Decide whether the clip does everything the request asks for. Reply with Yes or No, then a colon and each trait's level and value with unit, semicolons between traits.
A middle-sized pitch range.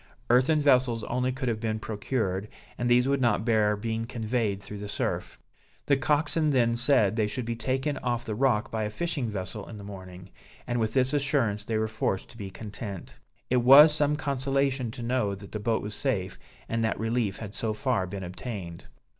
Yes: average, 3.7 semitones